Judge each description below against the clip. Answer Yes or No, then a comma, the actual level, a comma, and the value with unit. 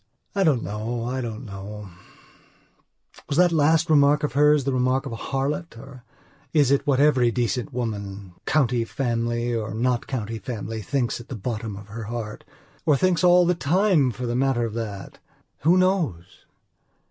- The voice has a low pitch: Yes, low, 125 Hz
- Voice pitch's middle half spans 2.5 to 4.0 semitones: No, average, 4.4 semitones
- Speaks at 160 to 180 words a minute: Yes, average, 170 wpm